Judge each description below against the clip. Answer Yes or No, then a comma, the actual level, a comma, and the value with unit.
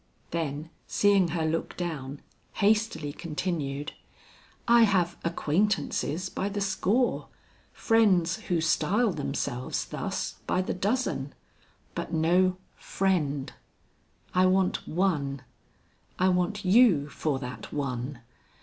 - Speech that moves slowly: Yes, slow, 105 wpm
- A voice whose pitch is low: No, medium, 175 Hz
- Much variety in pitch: No, average, 4.9 semitones